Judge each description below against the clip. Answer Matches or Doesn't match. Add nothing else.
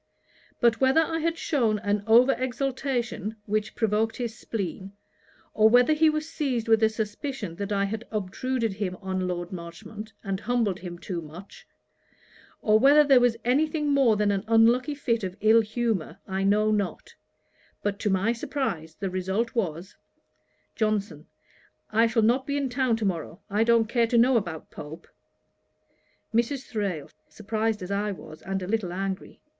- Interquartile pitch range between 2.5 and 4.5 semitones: Matches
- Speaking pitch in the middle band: Doesn't match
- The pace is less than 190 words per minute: Matches